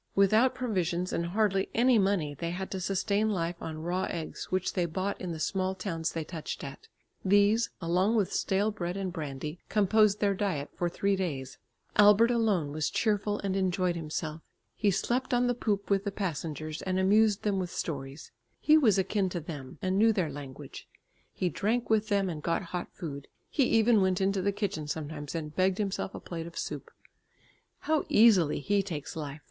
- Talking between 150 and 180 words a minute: No, average, 190 wpm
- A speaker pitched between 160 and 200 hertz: Yes, high, 190 Hz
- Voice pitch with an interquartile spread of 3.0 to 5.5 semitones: Yes, average, 3.9 semitones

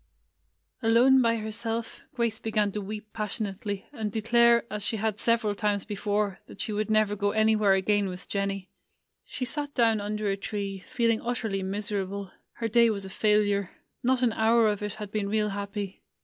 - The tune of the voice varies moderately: No, narrow, 2.1 semitones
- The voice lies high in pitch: Yes, high, 210 Hz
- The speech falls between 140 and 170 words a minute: No, average, 185 wpm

